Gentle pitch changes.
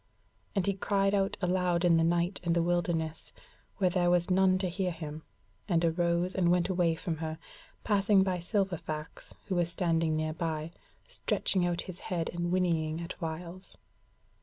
Yes: narrow, 2.0 semitones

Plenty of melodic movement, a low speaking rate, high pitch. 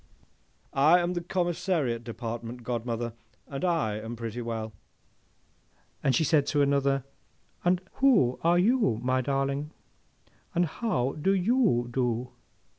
No: wide, 6.6 semitones; slow, 120 wpm; low, 135 Hz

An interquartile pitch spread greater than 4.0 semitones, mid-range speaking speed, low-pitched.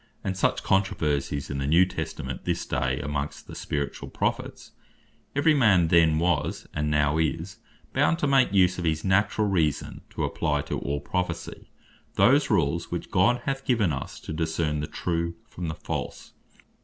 Yes: average, 4.6 semitones; average, 170 wpm; very low, 85 Hz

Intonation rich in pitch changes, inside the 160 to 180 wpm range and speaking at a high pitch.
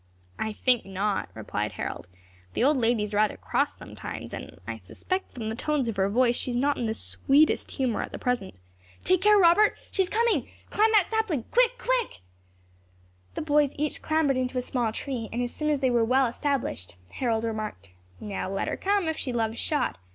No: wide, 5.9 semitones; fast, 205 wpm; very high, 255 Hz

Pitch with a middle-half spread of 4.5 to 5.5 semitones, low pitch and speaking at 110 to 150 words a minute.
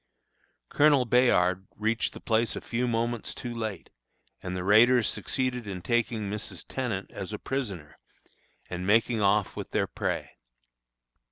No: average, 3.6 semitones; low, 110 Hz; average, 145 wpm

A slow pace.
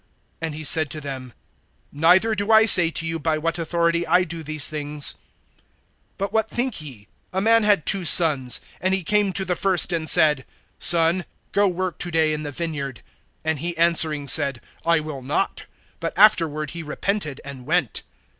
No: average, 185 wpm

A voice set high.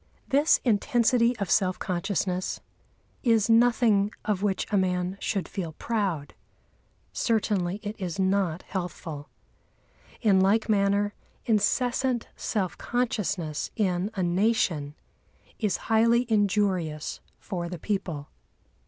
Yes: high, 200 Hz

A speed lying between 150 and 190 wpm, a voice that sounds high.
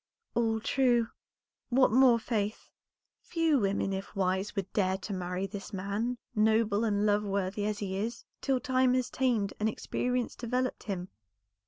Yes: average, 155 wpm; high, 215 Hz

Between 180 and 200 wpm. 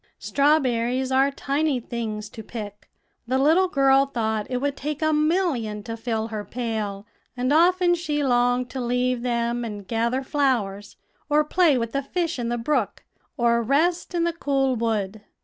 No: average, 165 wpm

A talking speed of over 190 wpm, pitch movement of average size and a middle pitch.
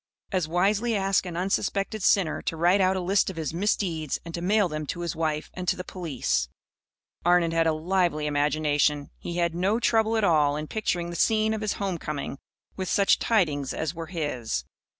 Yes: average, 200 wpm; average, 4.0 semitones; medium, 175 Hz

